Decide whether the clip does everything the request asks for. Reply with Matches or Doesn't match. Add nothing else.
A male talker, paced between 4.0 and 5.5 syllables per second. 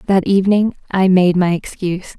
Doesn't match